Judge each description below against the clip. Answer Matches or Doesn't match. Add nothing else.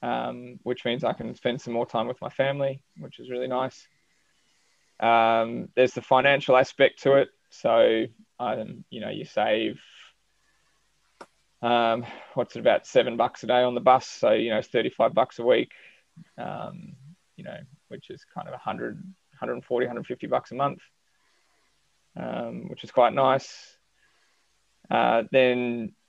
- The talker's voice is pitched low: Matches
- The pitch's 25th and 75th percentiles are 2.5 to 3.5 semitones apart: Matches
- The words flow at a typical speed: Matches